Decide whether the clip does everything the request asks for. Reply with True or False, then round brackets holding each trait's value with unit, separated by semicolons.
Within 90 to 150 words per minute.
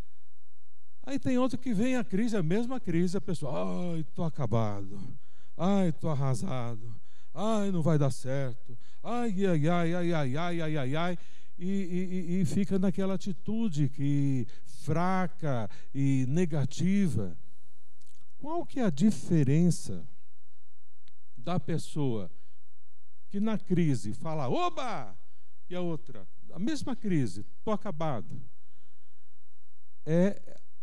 True (120 wpm)